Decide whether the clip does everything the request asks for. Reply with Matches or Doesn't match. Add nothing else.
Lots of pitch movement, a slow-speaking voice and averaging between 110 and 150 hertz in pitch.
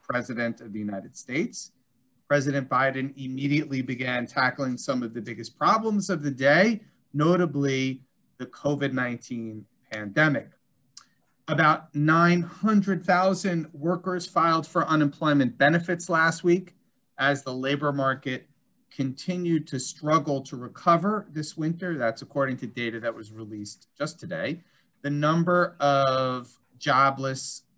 Doesn't match